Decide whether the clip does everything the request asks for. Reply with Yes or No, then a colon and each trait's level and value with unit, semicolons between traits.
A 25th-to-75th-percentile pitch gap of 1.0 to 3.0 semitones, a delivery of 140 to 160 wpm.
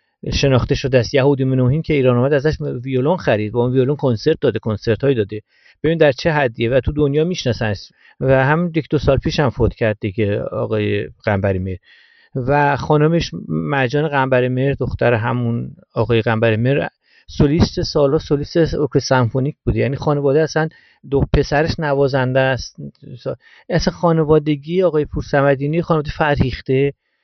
No: average, 4.0 semitones; average, 150 wpm